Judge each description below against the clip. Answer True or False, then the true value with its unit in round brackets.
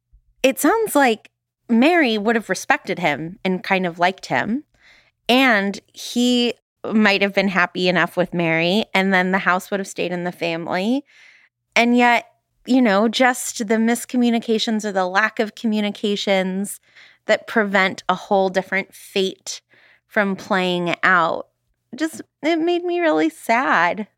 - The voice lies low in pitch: False (205 Hz)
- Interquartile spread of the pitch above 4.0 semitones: True (4.6 semitones)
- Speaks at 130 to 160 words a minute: True (145 wpm)